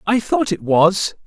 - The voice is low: No, high, 190 Hz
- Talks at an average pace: Yes, average, 190 wpm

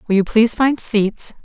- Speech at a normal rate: No, fast, 210 wpm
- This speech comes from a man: No, female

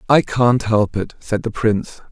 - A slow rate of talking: No, average, 200 wpm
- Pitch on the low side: Yes, low, 115 Hz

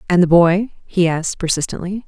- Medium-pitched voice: Yes, medium, 175 Hz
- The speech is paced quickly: No, average, 175 wpm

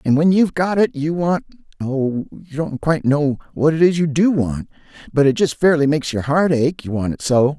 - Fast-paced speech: Yes, fast, 230 wpm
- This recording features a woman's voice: No, male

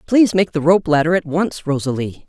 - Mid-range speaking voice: Yes, medium, 165 Hz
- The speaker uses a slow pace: No, fast, 210 wpm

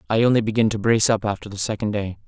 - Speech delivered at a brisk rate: Yes, fast, 265 wpm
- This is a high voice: No, low, 105 Hz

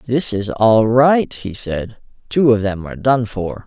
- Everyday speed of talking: Yes, average, 195 wpm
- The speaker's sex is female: No, male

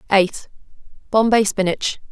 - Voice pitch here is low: No, high, 205 Hz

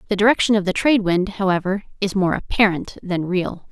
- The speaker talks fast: No, average, 195 wpm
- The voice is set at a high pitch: Yes, high, 195 Hz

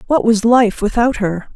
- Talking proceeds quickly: No, average, 195 wpm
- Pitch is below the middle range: No, high, 225 Hz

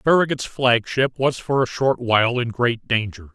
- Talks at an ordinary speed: Yes, average, 195 wpm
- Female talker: No, male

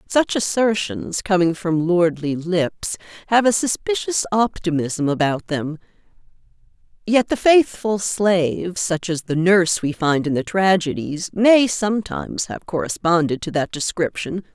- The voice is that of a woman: Yes, female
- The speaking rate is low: Yes, slow, 130 wpm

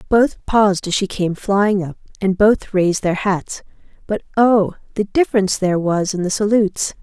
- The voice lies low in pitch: No, high, 195 Hz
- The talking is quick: No, average, 180 wpm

